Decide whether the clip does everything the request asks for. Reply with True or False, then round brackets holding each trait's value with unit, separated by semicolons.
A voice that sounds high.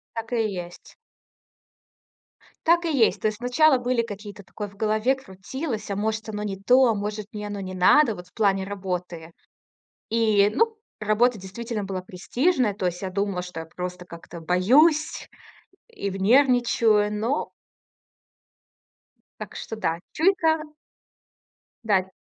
True (210 Hz)